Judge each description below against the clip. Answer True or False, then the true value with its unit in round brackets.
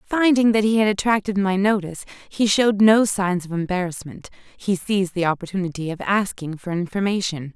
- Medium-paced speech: True (160 wpm)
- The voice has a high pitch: True (195 Hz)